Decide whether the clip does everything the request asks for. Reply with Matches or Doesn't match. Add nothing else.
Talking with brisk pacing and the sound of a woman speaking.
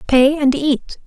Doesn't match